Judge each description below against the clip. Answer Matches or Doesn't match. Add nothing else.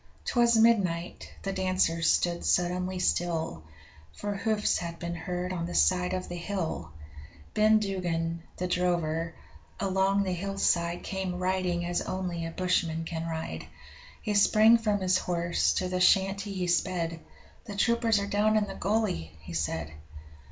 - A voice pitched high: Doesn't match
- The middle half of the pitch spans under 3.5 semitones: Matches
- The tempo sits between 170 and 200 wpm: Doesn't match